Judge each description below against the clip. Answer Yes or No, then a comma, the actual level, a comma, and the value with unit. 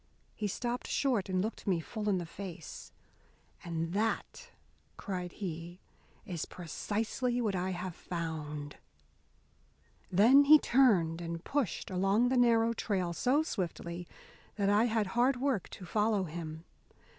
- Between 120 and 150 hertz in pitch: No, high, 195 Hz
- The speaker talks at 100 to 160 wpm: Yes, slow, 135 wpm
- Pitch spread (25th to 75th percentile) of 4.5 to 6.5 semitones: Yes, average, 5.2 semitones